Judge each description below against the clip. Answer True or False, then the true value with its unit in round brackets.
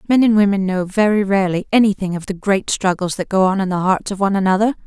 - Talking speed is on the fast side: True (245 wpm)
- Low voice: False (195 Hz)